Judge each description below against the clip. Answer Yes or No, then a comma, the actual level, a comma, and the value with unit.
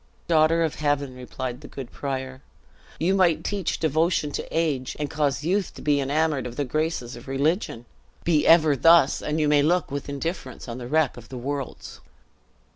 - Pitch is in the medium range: Yes, medium, 145 Hz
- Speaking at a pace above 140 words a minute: Yes, average, 180 wpm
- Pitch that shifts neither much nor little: Yes, average, 3.4 semitones